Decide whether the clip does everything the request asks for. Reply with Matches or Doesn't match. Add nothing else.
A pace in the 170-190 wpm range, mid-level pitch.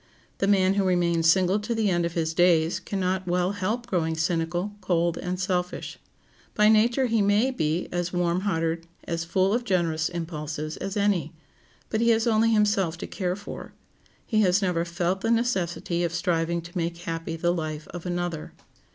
Matches